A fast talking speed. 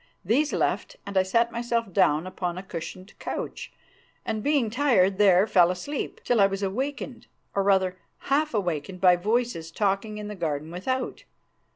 No: average, 165 wpm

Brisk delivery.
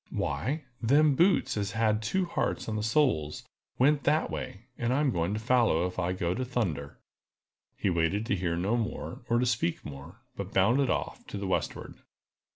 No: average, 185 wpm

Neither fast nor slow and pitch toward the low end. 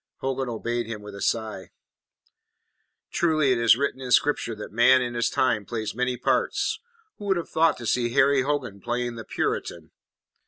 Yes: average, 180 wpm; low, 120 Hz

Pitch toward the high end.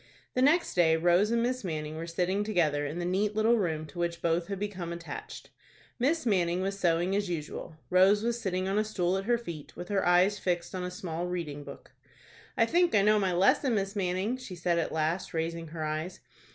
No: medium, 180 Hz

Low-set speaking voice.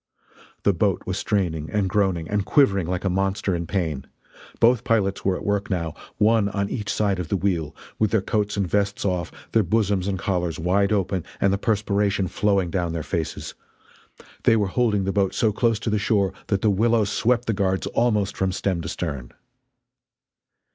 Yes: low, 100 Hz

